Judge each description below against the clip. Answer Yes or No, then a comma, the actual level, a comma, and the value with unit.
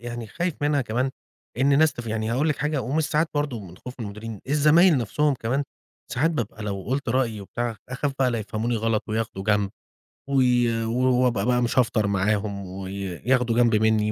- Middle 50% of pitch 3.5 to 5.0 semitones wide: Yes, average, 4.0 semitones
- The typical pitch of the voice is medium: No, low, 120 Hz